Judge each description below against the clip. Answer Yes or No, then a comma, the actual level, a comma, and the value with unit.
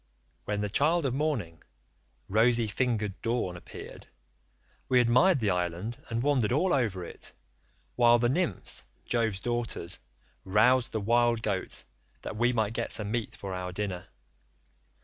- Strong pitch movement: No, average, 3.5 semitones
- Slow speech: No, average, 145 wpm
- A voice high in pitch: No, low, 115 Hz